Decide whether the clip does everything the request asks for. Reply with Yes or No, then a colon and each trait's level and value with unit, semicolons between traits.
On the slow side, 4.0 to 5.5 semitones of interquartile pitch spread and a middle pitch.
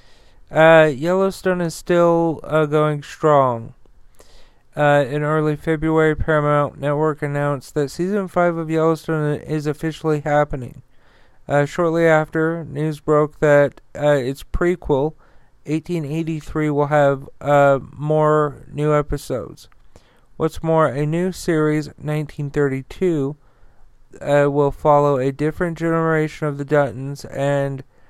No: slow, 115 wpm; narrow, 2.0 semitones; medium, 150 Hz